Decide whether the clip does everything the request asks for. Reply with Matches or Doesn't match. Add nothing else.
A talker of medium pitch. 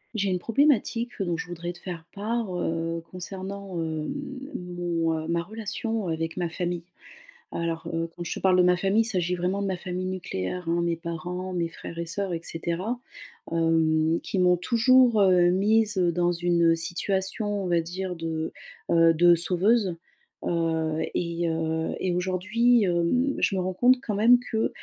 Matches